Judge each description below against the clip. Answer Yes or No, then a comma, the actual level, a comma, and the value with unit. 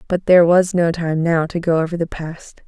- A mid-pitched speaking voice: Yes, medium, 170 Hz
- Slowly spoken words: No, fast, 245 wpm